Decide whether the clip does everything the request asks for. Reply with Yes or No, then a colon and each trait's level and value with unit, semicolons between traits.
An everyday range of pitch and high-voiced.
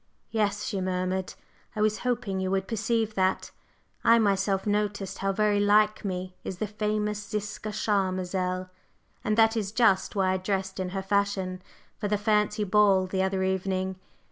No: narrow, 2.0 semitones; high, 200 Hz